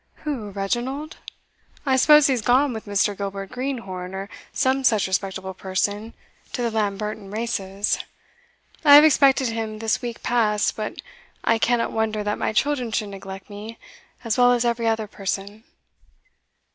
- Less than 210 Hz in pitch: No, high, 220 Hz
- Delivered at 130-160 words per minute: Yes, average, 150 wpm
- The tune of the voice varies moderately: Yes, average, 3.5 semitones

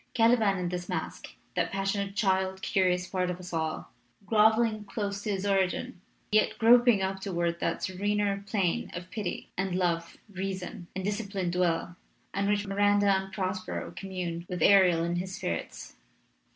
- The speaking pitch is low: No, high, 190 Hz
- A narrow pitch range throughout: Yes, narrow, 2.1 semitones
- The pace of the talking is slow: No, average, 165 wpm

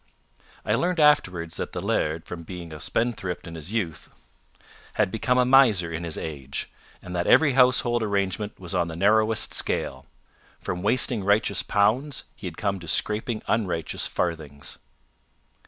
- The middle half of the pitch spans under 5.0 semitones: No, average, 5.3 semitones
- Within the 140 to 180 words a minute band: Yes, average, 155 wpm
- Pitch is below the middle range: Yes, low, 100 Hz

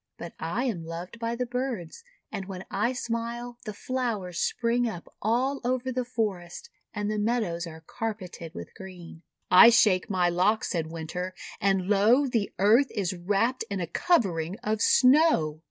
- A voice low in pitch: No, high, 210 Hz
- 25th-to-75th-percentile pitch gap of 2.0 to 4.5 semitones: No, average, 5.1 semitones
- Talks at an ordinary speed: Yes, average, 165 wpm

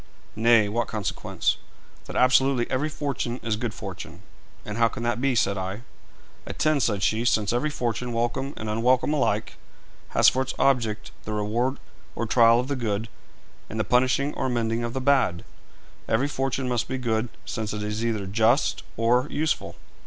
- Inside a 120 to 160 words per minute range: No, average, 175 wpm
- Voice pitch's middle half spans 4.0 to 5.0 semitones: No, average, 2.9 semitones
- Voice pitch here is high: No, low, 120 Hz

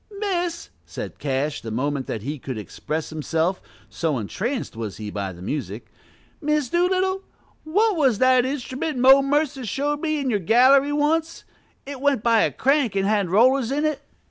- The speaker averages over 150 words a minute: Yes, average, 170 wpm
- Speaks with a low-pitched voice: No, very high, 255 Hz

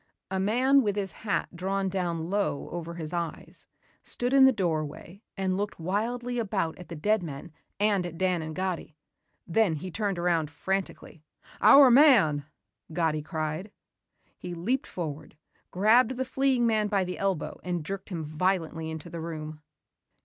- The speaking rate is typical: Yes, average, 160 wpm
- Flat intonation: No, average, 4.3 semitones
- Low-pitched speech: No, medium, 185 Hz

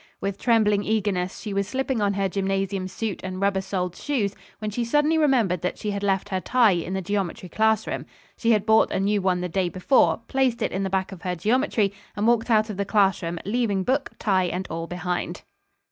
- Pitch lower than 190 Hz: No, high, 200 Hz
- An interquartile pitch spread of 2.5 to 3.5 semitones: Yes, average, 2.8 semitones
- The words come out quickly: Yes, fast, 215 wpm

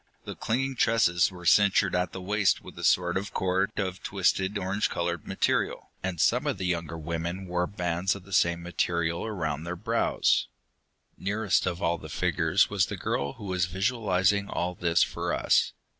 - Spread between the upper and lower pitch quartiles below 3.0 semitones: Yes, narrow, 2.5 semitones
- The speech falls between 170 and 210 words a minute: Yes, average, 180 wpm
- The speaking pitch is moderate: No, very low, 90 Hz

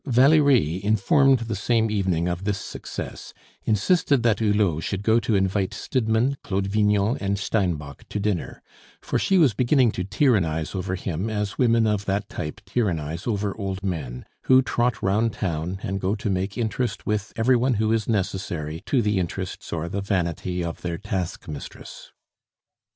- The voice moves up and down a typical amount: Yes, average, 3.6 semitones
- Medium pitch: No, low, 100 Hz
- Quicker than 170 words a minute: No, average, 165 wpm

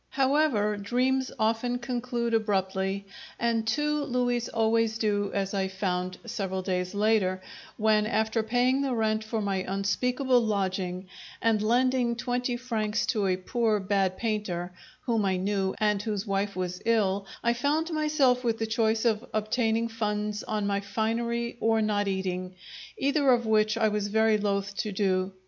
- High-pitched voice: Yes, high, 220 Hz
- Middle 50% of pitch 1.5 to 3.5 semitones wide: Yes, average, 3.1 semitones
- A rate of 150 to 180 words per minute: Yes, average, 155 wpm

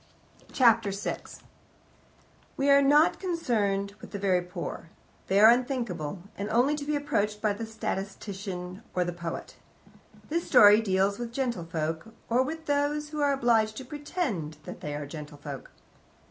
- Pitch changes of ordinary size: No, wide, 6.9 semitones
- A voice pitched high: Yes, high, 215 Hz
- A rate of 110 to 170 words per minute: Yes, average, 150 wpm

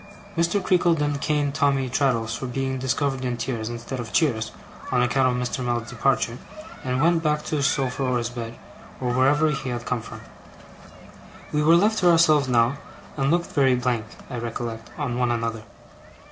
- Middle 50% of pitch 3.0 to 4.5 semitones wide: Yes, average, 3.5 semitones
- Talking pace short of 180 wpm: No, average, 185 wpm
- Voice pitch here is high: No, low, 130 Hz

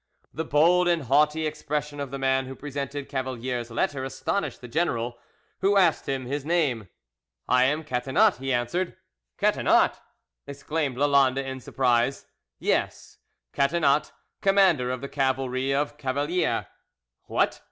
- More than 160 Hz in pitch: No, medium, 140 Hz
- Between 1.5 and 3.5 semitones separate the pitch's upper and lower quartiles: Yes, average, 2.8 semitones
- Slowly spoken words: Yes, slow, 130 wpm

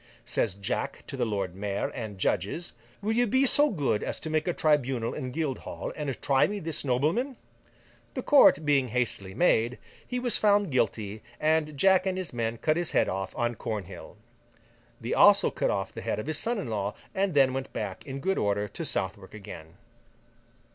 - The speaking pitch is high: No, low, 135 Hz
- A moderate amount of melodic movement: No, wide, 8.3 semitones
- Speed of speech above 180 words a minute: Yes, average, 190 wpm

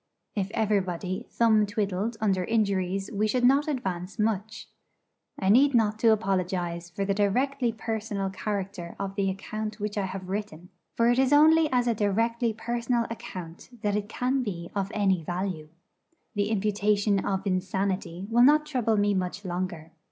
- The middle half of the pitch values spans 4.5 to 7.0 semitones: No, average, 3.2 semitones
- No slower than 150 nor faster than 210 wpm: Yes, average, 160 wpm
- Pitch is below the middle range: No, high, 205 Hz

